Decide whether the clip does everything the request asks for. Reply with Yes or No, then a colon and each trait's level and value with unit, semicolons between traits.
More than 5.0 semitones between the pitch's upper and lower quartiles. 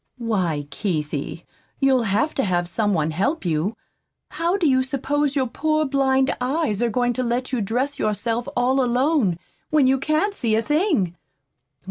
Yes: wide, 5.4 semitones